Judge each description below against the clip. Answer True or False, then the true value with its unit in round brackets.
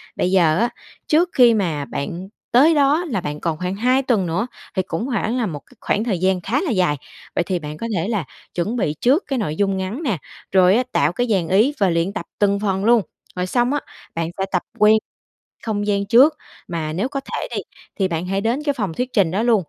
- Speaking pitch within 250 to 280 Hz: False (200 Hz)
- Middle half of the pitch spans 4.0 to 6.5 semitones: True (5.2 semitones)